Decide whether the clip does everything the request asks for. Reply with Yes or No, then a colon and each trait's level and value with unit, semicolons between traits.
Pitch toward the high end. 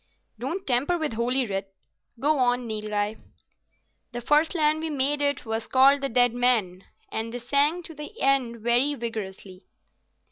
Yes: high, 245 Hz